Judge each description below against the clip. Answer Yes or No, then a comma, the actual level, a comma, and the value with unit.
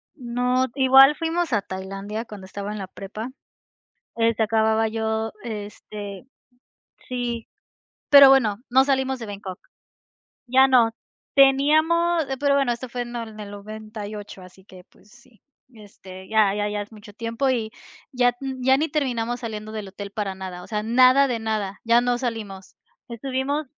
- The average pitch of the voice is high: Yes, high, 225 Hz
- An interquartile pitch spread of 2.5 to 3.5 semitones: No, average, 3.9 semitones